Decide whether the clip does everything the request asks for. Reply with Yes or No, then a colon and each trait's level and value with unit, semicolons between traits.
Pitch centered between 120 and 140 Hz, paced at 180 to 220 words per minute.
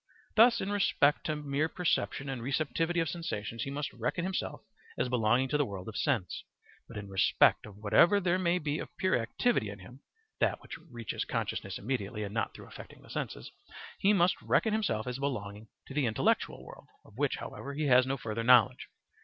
Yes: low, 135 Hz; average, 195 wpm